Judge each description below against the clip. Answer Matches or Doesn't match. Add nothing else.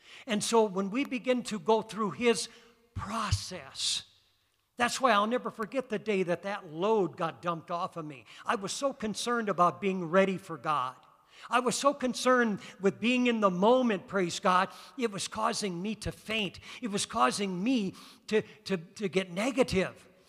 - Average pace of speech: Matches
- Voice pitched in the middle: Doesn't match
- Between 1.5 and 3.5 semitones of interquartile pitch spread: Doesn't match